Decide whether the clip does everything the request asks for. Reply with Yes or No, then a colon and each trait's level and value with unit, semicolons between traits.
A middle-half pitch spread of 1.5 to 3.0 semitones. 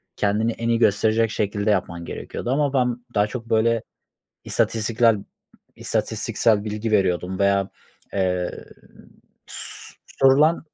Yes: average, 2.7 semitones